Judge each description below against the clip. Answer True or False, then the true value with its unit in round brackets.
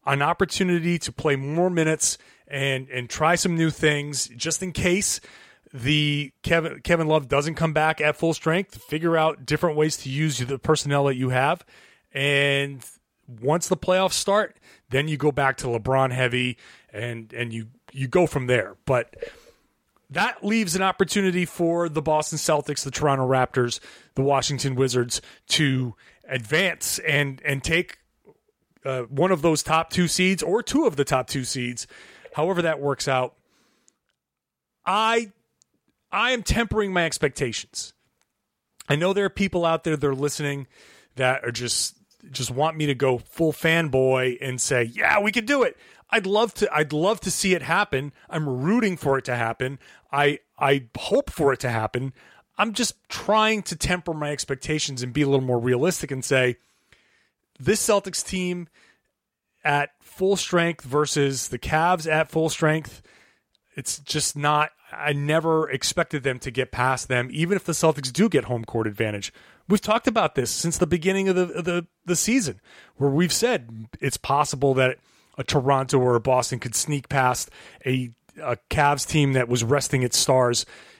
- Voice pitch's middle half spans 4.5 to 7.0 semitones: True (4.9 semitones)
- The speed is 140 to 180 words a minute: True (170 wpm)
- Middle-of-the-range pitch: True (150 Hz)